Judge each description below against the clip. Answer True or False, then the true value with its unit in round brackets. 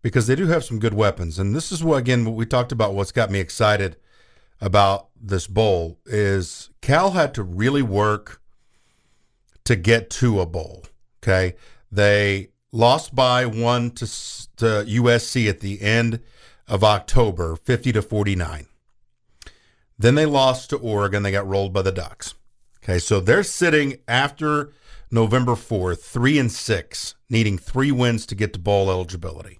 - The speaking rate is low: False (160 wpm)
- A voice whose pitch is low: True (110 Hz)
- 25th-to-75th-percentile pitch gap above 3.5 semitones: True (3.9 semitones)